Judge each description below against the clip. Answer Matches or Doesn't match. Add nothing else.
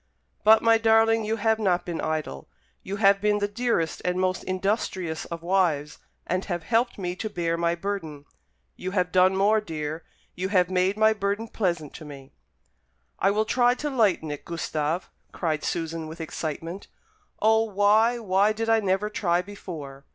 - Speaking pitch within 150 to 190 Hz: Matches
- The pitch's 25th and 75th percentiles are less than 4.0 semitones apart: Doesn't match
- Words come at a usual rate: Matches